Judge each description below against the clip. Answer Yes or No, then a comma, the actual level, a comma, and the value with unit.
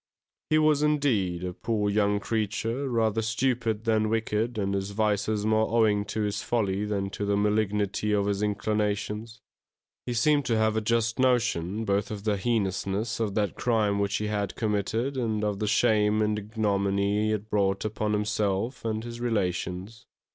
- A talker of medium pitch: No, low, 105 Hz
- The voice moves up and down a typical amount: No, narrow, 1.8 semitones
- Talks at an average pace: Yes, average, 170 wpm